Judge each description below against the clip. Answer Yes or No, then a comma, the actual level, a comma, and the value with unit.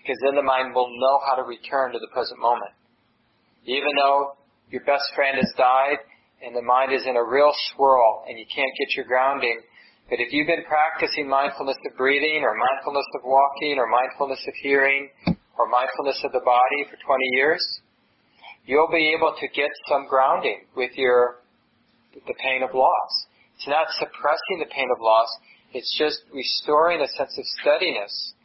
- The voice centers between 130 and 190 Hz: Yes, low, 135 Hz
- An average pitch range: No, narrow, 2.0 semitones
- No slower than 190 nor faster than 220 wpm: No, average, 180 wpm